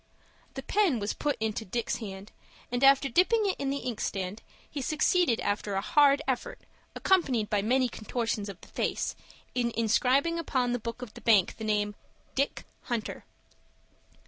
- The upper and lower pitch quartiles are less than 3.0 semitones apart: No, average, 4.6 semitones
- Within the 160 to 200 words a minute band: Yes, average, 165 wpm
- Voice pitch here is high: Yes, high, 245 Hz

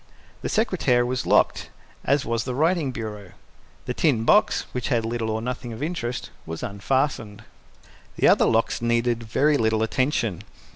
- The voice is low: Yes, low, 120 Hz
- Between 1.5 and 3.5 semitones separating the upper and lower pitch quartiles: Yes, average, 3.2 semitones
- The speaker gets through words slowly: No, average, 155 wpm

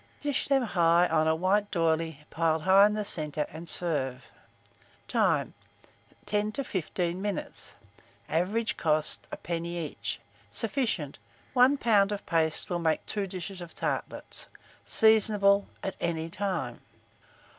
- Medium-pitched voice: Yes, medium, 175 Hz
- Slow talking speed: Yes, slow, 130 wpm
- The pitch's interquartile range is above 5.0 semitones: No, average, 4.3 semitones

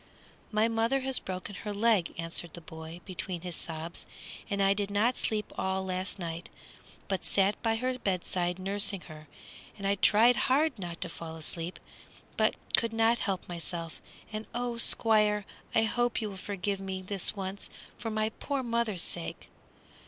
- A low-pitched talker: No, high, 200 Hz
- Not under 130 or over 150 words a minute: No, average, 165 wpm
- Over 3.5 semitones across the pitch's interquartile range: Yes, average, 4.0 semitones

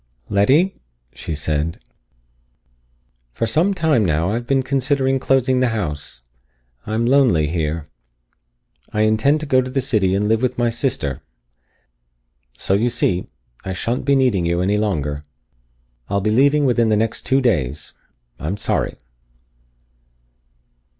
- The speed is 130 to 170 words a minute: Yes, average, 140 wpm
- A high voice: No, low, 110 Hz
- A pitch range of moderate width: No, wide, 6.7 semitones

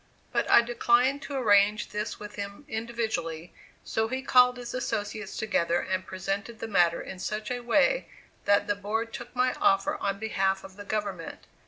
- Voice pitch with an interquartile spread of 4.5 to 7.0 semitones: No, average, 3.4 semitones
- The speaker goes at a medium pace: Yes, average, 175 wpm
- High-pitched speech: Yes, high, 215 Hz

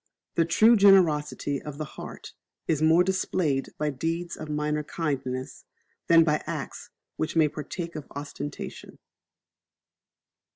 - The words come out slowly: Yes, slow, 125 wpm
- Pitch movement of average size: No, narrow, 2.3 semitones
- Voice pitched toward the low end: No, medium, 155 Hz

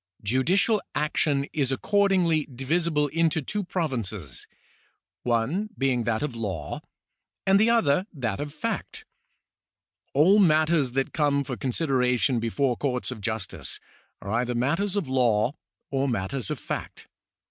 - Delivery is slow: Yes, slow, 130 wpm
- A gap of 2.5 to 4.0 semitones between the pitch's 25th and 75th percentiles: No, wide, 5.4 semitones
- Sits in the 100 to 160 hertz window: Yes, medium, 140 Hz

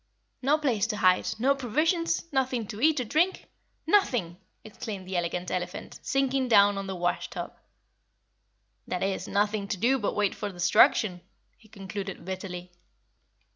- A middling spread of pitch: No, wide, 5.9 semitones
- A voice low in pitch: No, high, 210 Hz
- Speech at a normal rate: Yes, average, 150 wpm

